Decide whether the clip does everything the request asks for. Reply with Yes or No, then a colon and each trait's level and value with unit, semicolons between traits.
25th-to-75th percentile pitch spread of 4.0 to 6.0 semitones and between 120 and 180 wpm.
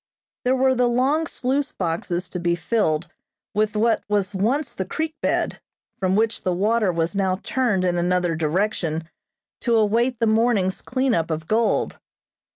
Yes: average, 5.1 semitones; average, 160 wpm